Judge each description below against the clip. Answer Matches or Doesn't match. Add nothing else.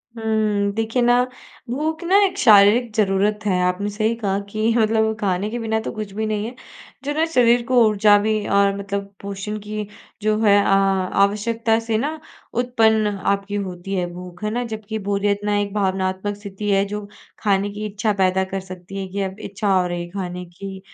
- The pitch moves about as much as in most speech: Doesn't match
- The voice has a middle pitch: Doesn't match